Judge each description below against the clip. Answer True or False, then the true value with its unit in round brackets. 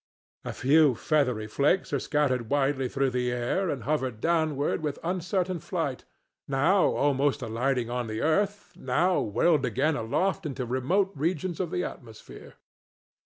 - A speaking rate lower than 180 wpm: True (145 wpm)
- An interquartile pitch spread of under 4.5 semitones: False (5.1 semitones)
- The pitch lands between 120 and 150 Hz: True (140 Hz)